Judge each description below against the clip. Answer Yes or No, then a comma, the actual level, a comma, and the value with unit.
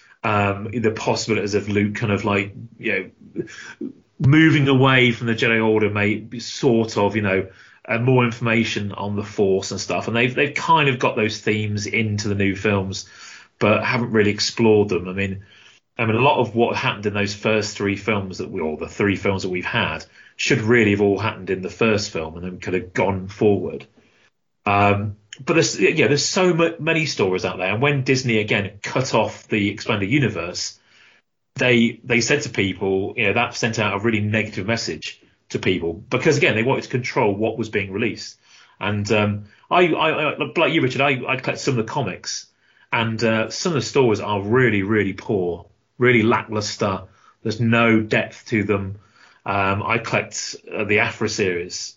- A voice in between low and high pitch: No, low, 105 Hz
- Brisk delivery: No, average, 195 wpm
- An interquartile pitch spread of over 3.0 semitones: No, narrow, 2.6 semitones